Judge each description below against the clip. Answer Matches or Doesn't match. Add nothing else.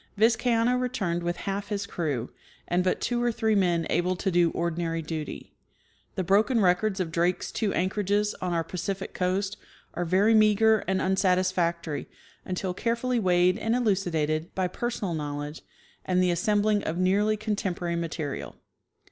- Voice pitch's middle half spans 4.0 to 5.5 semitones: Doesn't match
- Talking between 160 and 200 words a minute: Doesn't match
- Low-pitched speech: Doesn't match